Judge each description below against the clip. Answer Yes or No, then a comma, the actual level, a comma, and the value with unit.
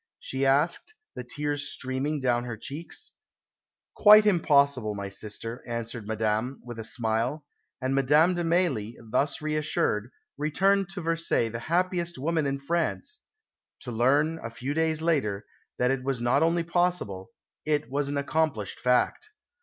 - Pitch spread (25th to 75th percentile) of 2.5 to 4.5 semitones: No, wide, 5.4 semitones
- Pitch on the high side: No, medium, 140 Hz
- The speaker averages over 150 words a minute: No, average, 145 wpm